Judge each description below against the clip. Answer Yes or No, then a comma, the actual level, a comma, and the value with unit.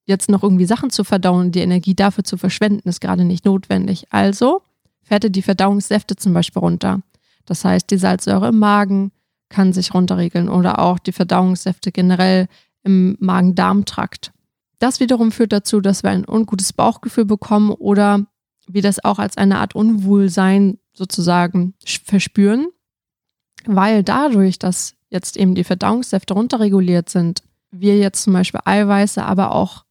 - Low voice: No, high, 195 Hz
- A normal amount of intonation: No, narrow, 1.9 semitones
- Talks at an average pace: Yes, average, 150 wpm